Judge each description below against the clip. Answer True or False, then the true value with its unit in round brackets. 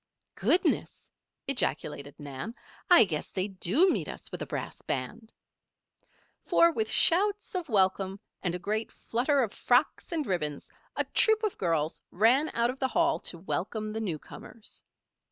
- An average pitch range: False (8.1 semitones)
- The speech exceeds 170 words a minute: False (155 wpm)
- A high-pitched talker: True (220 Hz)